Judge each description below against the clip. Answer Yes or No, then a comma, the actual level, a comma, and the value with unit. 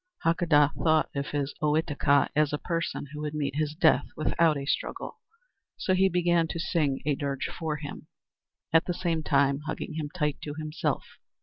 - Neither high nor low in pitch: Yes, medium, 150 Hz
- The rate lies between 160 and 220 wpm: Yes, average, 180 wpm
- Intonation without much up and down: Yes, narrow, 2.2 semitones